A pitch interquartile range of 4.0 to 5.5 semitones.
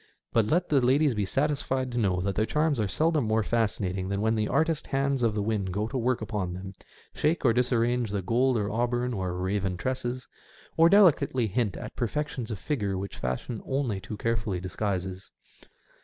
Yes: average, 4.7 semitones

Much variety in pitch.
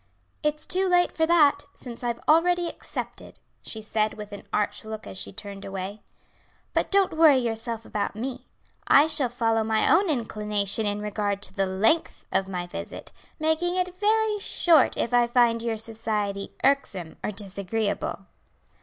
Yes: wide, 7.0 semitones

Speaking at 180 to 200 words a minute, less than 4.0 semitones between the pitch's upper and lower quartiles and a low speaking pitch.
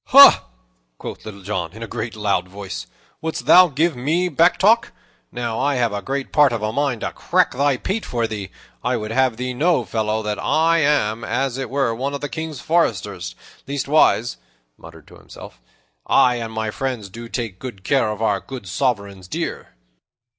No: average, 190 wpm; average, 4.8 semitones; low, 120 Hz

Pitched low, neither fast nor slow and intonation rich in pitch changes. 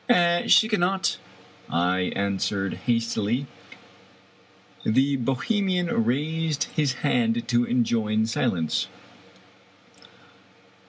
No: low, 120 Hz; slow, 70 wpm; wide, 5.9 semitones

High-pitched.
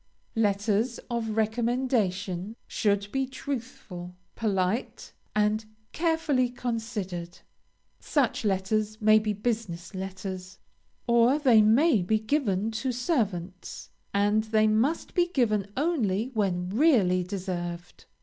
Yes: high, 215 Hz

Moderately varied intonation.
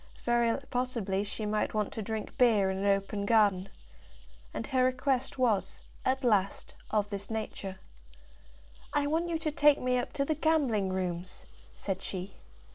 Yes: average, 4.6 semitones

